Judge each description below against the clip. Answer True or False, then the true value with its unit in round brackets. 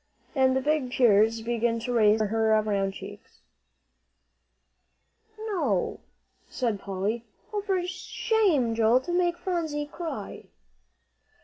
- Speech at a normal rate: False (115 wpm)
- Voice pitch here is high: True (245 Hz)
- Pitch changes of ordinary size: False (7.7 semitones)